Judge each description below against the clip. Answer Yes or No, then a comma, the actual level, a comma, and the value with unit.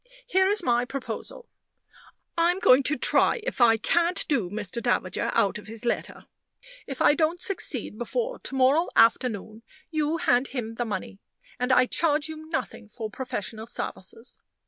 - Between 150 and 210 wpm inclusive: Yes, average, 160 wpm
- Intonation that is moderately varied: No, wide, 6.3 semitones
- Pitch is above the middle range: Yes, very high, 255 Hz